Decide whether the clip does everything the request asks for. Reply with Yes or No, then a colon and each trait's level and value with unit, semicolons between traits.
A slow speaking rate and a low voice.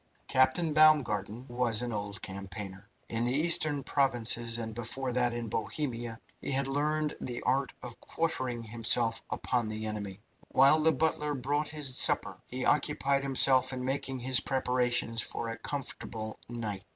No: average, 150 wpm; low, 125 Hz